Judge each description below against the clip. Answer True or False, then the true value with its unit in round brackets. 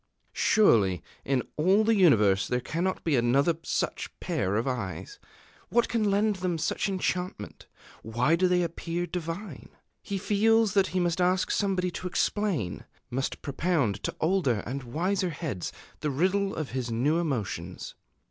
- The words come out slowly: False (150 wpm)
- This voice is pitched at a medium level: True (170 Hz)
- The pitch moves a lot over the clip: True (7.1 semitones)